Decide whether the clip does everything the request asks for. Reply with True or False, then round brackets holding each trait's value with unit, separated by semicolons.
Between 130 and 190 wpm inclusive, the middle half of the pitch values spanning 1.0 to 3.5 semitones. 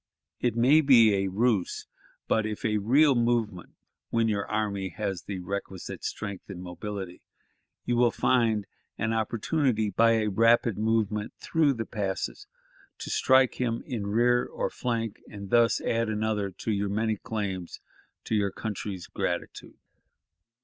True (150 wpm; 2.7 semitones)